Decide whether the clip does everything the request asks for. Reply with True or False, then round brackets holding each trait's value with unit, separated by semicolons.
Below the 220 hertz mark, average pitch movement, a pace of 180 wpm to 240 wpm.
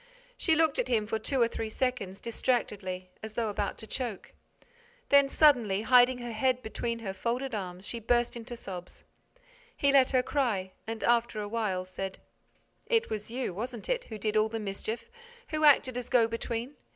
False (230 Hz; 3.3 semitones; 185 wpm)